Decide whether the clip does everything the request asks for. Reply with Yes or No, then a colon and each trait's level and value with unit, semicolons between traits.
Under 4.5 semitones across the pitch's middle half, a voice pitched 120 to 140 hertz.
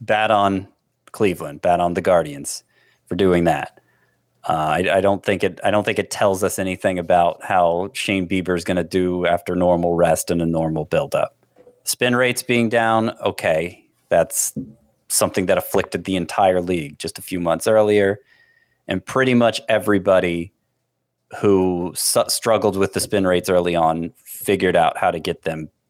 No: average, 3.4 semitones; very low, 95 Hz